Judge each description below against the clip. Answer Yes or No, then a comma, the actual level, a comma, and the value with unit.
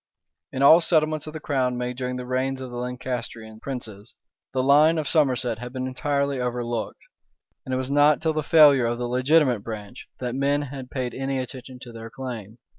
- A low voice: Yes, low, 130 Hz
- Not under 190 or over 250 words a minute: Yes, average, 200 wpm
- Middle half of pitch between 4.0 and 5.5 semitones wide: No, narrow, 2.5 semitones